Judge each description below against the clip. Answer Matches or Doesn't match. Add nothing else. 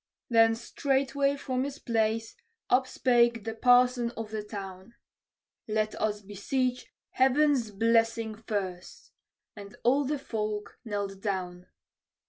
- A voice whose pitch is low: Doesn't match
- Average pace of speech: Doesn't match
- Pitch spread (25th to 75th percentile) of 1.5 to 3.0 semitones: Doesn't match